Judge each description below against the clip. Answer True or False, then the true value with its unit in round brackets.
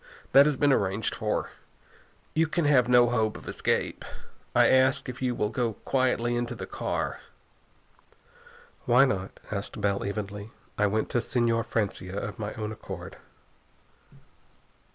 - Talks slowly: False (150 wpm)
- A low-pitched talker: True (120 Hz)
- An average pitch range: True (3.8 semitones)